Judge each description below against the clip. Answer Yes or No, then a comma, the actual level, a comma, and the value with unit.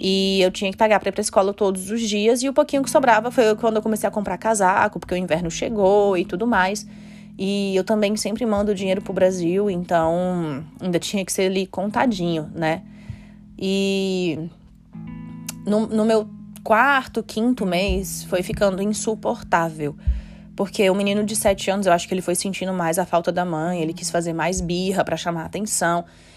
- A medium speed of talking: No, fast, 190 wpm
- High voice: Yes, high, 195 Hz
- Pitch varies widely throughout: No, average, 2.9 semitones